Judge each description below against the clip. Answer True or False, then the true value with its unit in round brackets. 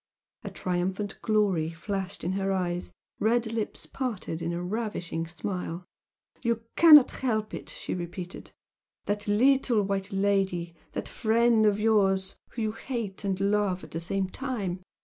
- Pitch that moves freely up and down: False (3.3 semitones)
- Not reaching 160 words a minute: True (150 wpm)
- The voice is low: False (195 Hz)